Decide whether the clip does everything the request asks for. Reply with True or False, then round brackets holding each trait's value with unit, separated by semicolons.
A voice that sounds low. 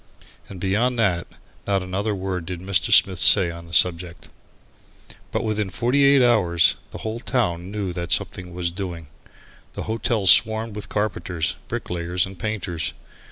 True (95 Hz)